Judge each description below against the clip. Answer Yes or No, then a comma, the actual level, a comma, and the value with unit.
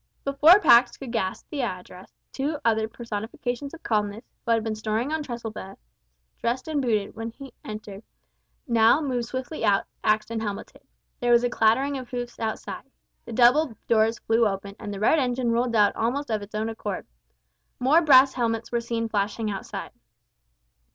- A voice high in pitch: Yes, high, 230 Hz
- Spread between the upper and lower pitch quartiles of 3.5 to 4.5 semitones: No, average, 3.0 semitones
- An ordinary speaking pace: Yes, average, 175 wpm